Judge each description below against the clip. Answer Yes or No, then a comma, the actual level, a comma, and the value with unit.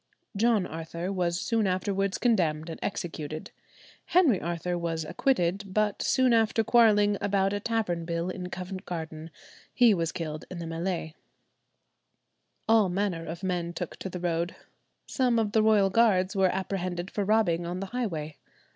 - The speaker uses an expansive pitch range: No, average, 3.5 semitones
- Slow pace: No, average, 155 wpm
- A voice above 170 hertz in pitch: Yes, medium, 185 Hz